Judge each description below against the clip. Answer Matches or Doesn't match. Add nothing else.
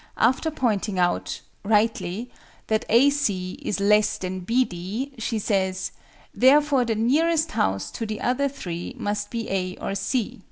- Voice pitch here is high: Matches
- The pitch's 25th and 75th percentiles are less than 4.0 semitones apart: Doesn't match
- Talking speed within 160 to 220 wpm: Doesn't match